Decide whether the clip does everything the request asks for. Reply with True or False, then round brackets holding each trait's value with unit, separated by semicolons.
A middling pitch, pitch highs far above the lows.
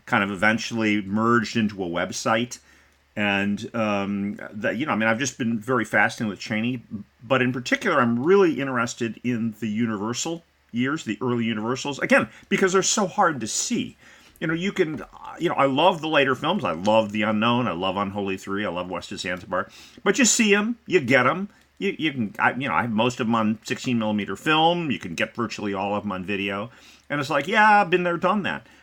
False (115 Hz; 8.1 semitones)